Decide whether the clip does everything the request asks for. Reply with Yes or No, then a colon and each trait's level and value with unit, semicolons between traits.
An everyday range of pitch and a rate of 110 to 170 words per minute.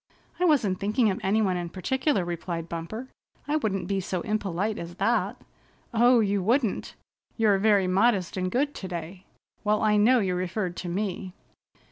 Yes: average, 3.3 semitones; average, 165 wpm